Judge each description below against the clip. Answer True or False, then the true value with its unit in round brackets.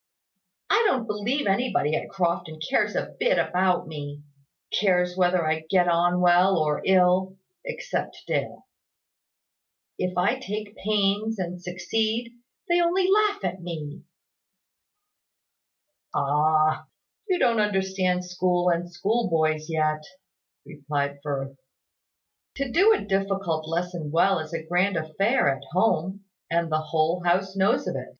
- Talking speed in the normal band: False (130 wpm)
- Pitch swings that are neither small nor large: True (4.1 semitones)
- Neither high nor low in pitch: True (180 Hz)